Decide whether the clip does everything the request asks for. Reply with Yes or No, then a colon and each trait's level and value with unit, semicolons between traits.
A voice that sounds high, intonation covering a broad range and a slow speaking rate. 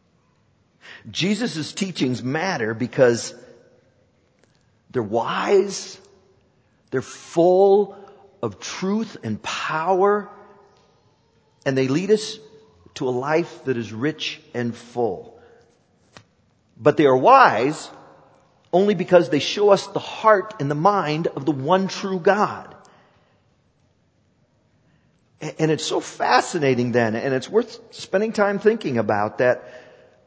No: medium, 165 Hz; wide, 7.2 semitones; slow, 110 wpm